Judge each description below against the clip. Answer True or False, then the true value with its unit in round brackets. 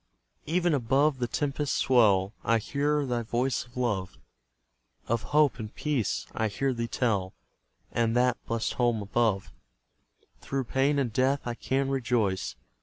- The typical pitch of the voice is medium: False (120 Hz)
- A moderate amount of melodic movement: True (3.4 semitones)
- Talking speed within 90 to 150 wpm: True (145 wpm)